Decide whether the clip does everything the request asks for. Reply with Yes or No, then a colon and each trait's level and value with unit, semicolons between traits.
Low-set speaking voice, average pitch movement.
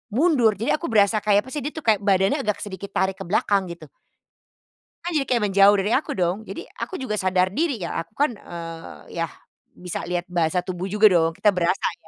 No: high, 195 Hz; average, 3.6 semitones